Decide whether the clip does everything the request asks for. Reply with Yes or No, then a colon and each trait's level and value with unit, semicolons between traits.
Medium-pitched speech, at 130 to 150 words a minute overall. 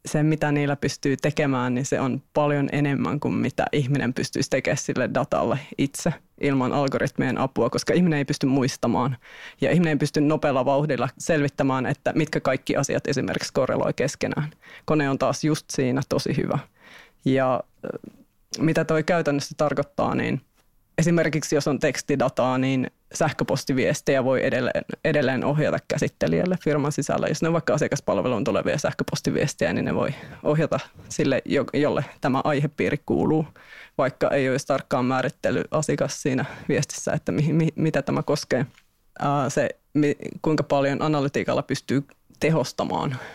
Yes: medium, 145 Hz; average, 140 wpm